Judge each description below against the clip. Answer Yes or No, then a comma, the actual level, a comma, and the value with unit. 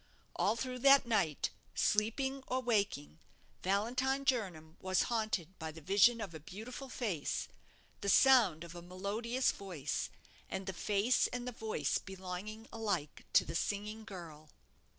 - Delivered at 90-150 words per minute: Yes, average, 145 wpm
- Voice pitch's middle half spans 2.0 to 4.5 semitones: No, average, 5.1 semitones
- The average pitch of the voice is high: Yes, high, 205 Hz